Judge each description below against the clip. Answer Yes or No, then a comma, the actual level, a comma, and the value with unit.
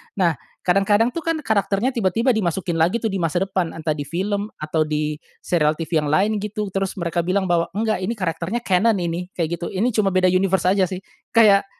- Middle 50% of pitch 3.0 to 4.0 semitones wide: Yes, average, 3.6 semitones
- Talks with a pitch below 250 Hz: Yes, medium, 185 Hz